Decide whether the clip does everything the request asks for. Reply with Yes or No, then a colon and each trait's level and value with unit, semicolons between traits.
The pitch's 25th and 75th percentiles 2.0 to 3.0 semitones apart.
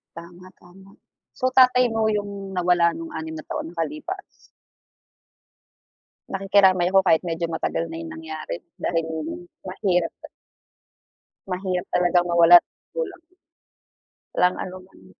Yes: average, 2.7 semitones